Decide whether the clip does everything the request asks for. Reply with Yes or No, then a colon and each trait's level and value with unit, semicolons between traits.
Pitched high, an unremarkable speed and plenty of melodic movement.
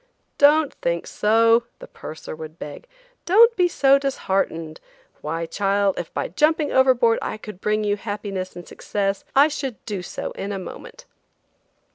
Yes: high, 210 Hz; average, 155 wpm; wide, 6.6 semitones